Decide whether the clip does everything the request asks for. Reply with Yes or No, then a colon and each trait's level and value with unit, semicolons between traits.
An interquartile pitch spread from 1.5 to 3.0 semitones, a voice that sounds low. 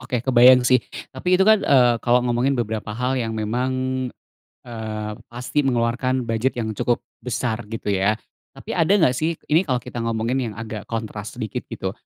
Yes: average, 2.7 semitones; low, 120 Hz